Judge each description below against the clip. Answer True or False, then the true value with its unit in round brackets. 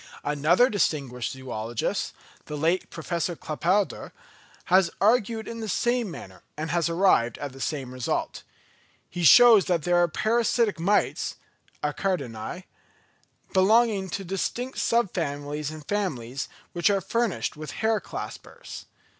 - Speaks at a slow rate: True (130 wpm)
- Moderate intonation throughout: False (6.0 semitones)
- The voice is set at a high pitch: False (175 Hz)